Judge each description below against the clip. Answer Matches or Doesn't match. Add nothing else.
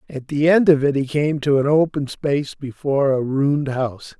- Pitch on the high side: Doesn't match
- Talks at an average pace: Doesn't match